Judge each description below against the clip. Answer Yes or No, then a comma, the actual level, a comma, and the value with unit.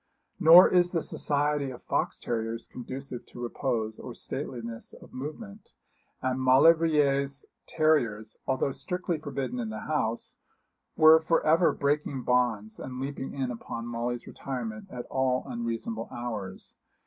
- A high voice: No, low, 130 Hz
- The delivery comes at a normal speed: No, slow, 130 wpm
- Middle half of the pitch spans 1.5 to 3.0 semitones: No, average, 4.2 semitones